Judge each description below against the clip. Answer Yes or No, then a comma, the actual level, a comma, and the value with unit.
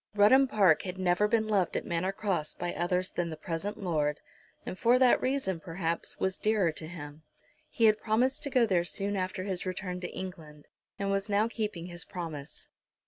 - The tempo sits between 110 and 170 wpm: No, average, 195 wpm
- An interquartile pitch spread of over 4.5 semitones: No, average, 3.6 semitones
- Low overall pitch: No, medium, 185 Hz